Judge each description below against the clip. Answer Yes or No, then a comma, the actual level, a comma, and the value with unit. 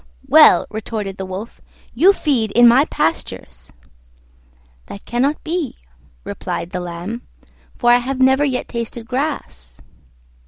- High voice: Yes, high, 235 Hz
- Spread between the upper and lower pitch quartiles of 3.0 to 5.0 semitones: No, wide, 5.6 semitones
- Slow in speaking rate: Yes, slow, 125 wpm